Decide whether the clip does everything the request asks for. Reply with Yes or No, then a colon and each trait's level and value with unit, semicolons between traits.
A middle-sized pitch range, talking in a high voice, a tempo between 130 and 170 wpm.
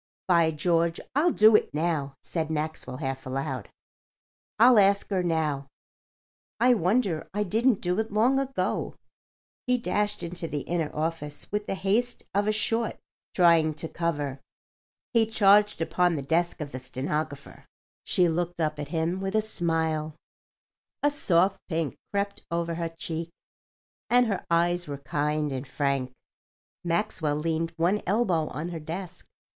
No: average, 4.6 semitones; medium, 170 Hz; average, 150 wpm